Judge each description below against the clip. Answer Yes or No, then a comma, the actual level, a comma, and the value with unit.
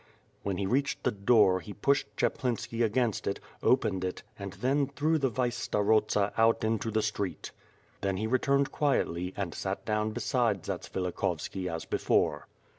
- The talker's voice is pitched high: No, low, 110 Hz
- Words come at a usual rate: Yes, average, 160 wpm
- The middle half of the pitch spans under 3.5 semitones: No, average, 4.2 semitones